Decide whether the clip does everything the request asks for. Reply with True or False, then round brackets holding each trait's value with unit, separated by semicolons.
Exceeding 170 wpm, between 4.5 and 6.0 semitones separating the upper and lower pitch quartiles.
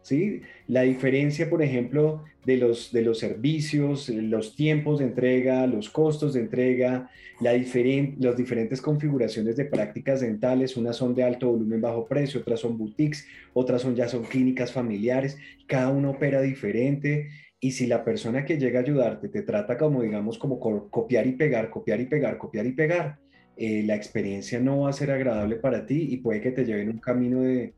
False (190 wpm; 3.1 semitones)